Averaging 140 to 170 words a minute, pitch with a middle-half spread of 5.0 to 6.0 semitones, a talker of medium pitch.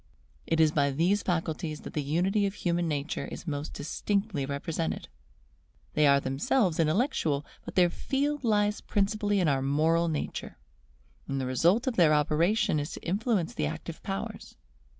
Yes: average, 160 wpm; wide, 5.5 semitones; medium, 165 Hz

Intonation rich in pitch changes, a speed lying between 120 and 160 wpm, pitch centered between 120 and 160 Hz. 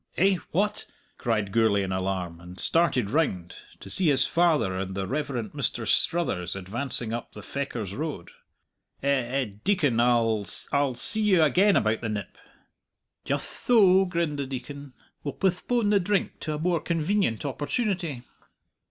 Yes: wide, 8.1 semitones; average, 150 wpm; medium, 140 Hz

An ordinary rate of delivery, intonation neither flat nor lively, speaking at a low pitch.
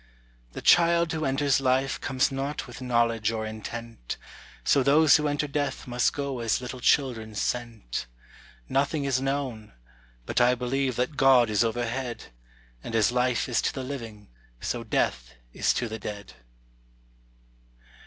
Yes: average, 150 wpm; average, 3.2 semitones; low, 125 Hz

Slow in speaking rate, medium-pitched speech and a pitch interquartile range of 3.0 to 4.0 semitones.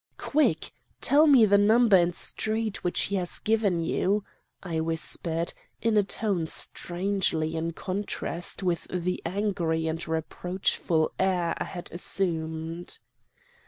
Yes: slow, 125 wpm; medium, 180 Hz; average, 3.6 semitones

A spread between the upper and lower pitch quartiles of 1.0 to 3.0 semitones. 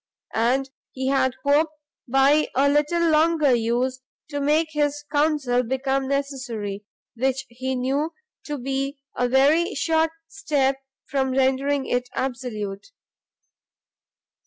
Yes: narrow, 2.4 semitones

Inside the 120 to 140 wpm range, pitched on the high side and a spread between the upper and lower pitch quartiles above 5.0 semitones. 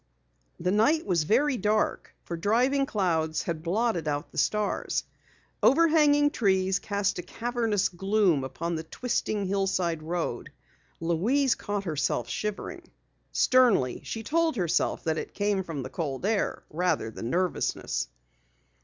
Yes: slow, 135 wpm; high, 195 Hz; wide, 5.5 semitones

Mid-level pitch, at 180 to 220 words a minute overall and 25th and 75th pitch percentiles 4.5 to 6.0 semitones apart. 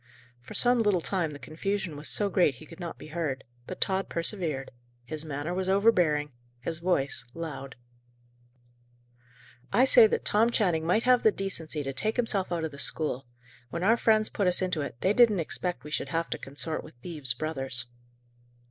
Yes: medium, 170 Hz; average, 185 wpm; average, 5.0 semitones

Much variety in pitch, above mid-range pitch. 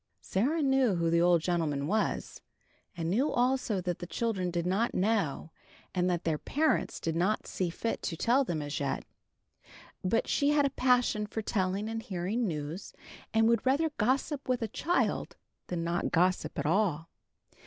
Yes: wide, 5.9 semitones; high, 195 Hz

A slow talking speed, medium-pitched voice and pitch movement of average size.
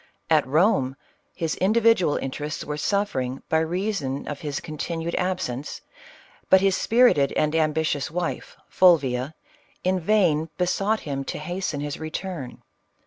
Yes: slow, 130 wpm; medium, 160 Hz; average, 4.3 semitones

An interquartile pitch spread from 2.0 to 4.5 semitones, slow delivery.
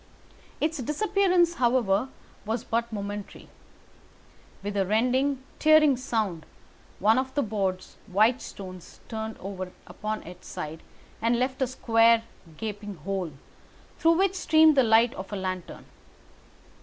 No: average, 4.9 semitones; slow, 130 wpm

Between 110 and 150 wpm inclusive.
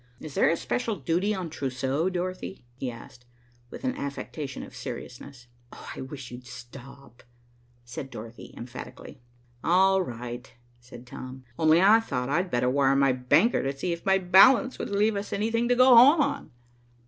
No: average, 165 wpm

